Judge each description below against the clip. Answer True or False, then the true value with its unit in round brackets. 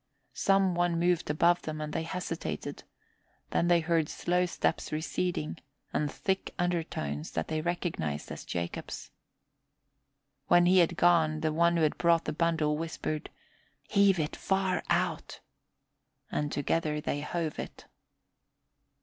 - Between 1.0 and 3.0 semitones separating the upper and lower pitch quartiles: True (2.4 semitones)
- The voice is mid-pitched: True (165 Hz)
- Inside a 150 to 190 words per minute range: False (135 wpm)